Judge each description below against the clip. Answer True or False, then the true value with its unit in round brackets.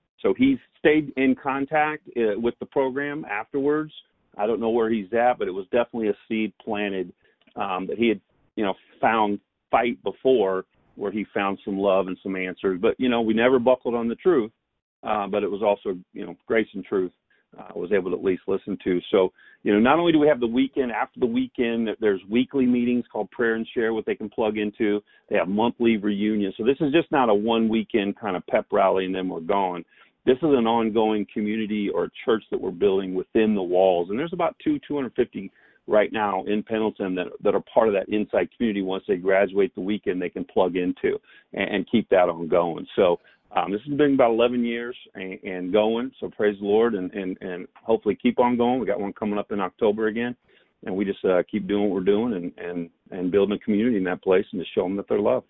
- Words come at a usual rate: False (230 wpm)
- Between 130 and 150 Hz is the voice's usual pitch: False (110 Hz)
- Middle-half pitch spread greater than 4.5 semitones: False (3.8 semitones)